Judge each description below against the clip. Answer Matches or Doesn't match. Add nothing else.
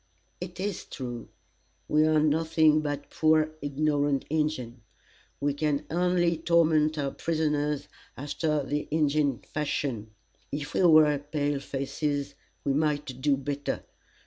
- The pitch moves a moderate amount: Doesn't match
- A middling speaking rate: Doesn't match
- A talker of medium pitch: Matches